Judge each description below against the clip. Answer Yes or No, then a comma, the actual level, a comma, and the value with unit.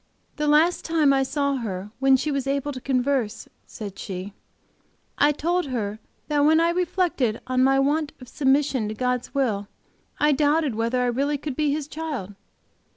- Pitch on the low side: No, very high, 275 Hz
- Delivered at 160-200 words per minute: Yes, average, 175 wpm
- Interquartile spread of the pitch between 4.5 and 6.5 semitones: No, average, 3.2 semitones